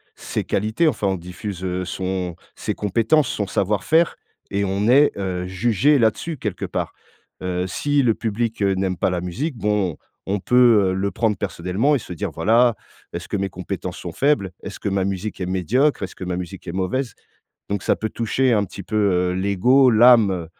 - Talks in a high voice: No, low, 100 Hz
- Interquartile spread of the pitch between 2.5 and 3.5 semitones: No, average, 4.1 semitones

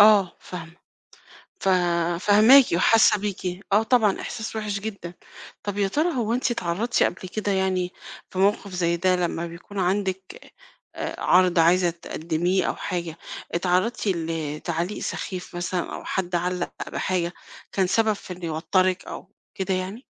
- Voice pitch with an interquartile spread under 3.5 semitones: Yes, average, 2.8 semitones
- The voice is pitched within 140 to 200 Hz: Yes, medium, 185 Hz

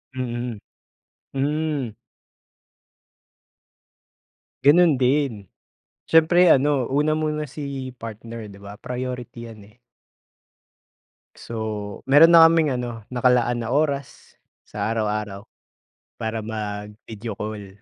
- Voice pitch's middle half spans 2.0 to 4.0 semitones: No, average, 4.8 semitones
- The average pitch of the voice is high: No, low, 125 Hz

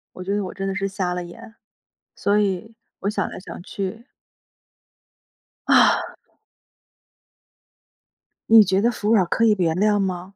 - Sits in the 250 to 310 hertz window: No, high, 195 Hz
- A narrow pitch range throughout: Yes, narrow, 2.3 semitones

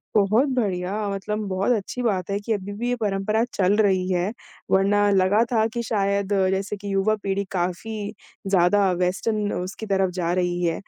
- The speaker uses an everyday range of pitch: No, narrow, 2.2 semitones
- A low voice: No, high, 200 Hz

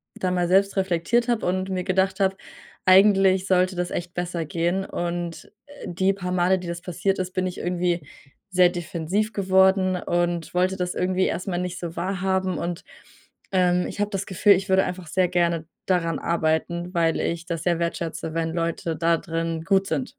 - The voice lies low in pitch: No, medium, 180 Hz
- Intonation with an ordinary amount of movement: No, narrow, 1.8 semitones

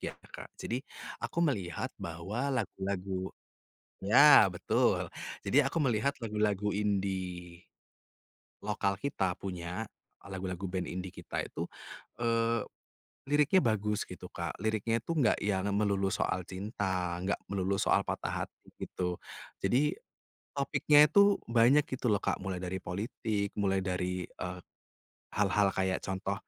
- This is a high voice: No, low, 100 Hz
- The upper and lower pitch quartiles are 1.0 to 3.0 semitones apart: No, average, 3.7 semitones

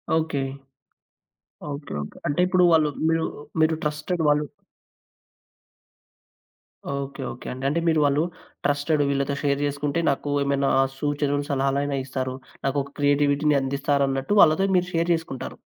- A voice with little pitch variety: Yes, narrow, 1.9 semitones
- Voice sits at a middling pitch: Yes, medium, 145 Hz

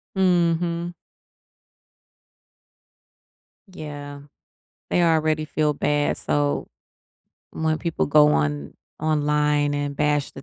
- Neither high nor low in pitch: Yes, medium, 150 Hz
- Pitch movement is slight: Yes, narrow, 1.6 semitones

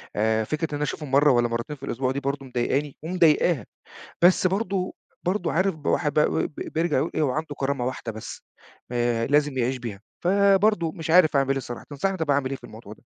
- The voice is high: No, medium, 145 Hz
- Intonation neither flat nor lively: Yes, average, 4.7 semitones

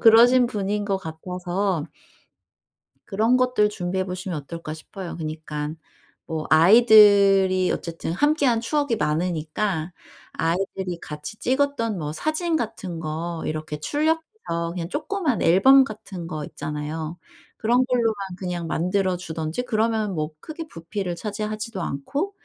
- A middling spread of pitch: No, wide, 5.7 semitones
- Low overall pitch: No, high, 190 Hz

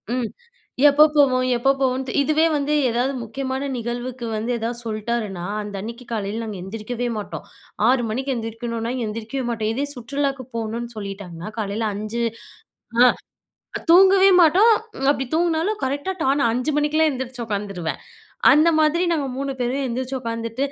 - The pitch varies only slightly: No, average, 3.7 semitones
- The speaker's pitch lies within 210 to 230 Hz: No, high, 245 Hz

